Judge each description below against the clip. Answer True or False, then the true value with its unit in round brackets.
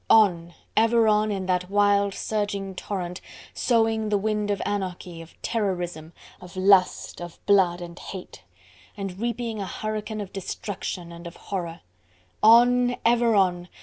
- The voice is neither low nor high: False (200 Hz)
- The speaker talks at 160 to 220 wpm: False (145 wpm)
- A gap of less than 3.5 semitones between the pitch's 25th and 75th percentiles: True (3.1 semitones)